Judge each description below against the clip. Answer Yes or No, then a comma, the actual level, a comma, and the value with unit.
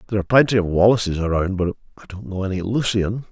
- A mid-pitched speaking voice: No, low, 100 Hz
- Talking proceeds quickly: Yes, fast, 215 wpm